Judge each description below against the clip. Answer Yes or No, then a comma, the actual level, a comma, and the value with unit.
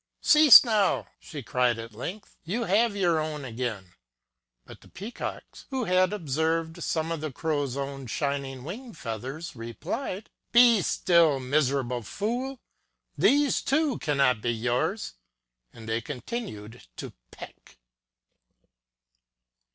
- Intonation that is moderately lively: No, wide, 8.4 semitones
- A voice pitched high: No, medium, 155 Hz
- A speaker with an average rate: No, slow, 125 wpm